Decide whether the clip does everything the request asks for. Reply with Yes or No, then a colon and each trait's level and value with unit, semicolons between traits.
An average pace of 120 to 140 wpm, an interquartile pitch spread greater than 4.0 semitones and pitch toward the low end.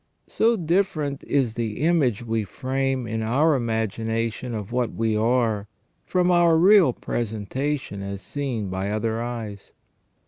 Yes: slow, 135 wpm; average, 4.6 semitones; low, 120 Hz